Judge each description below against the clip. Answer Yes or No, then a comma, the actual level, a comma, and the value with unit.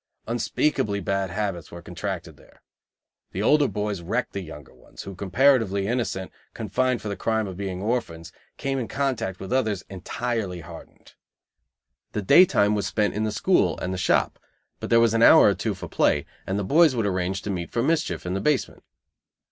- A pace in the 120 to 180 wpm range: No, average, 190 wpm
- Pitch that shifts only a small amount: No, average, 4.1 semitones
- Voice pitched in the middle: No, low, 105 Hz